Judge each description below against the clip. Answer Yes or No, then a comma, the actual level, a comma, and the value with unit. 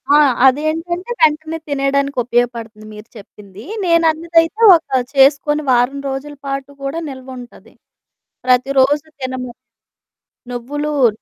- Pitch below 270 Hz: No, very high, 275 Hz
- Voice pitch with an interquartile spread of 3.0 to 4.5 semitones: Yes, average, 3.5 semitones